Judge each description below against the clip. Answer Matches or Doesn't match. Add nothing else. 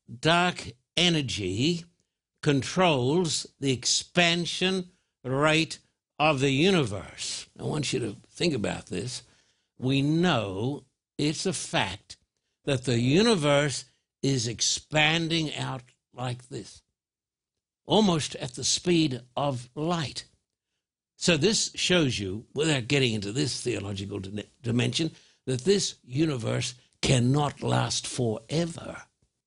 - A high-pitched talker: Doesn't match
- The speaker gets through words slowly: Matches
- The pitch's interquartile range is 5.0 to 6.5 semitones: Matches